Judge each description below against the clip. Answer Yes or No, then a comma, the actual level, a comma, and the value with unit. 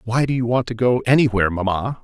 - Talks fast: Yes, fast, 235 wpm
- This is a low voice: Yes, low, 115 Hz